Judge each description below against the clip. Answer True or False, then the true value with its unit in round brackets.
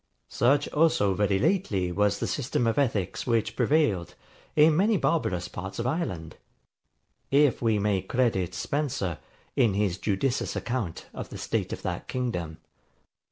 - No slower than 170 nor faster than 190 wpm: False (145 wpm)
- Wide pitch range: True (6.8 semitones)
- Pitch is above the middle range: False (115 Hz)